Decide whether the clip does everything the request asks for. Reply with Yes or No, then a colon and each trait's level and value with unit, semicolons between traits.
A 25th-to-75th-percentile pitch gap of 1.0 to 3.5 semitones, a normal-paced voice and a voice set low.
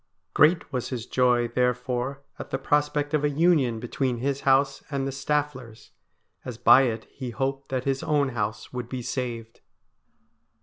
Yes: narrow, 2.5 semitones; average, 165 wpm; low, 130 Hz